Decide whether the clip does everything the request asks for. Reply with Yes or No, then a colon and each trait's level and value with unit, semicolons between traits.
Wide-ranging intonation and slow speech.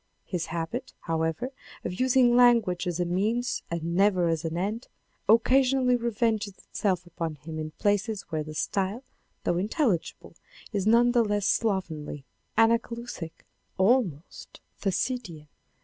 Yes: wide, 5.8 semitones; slow, 130 wpm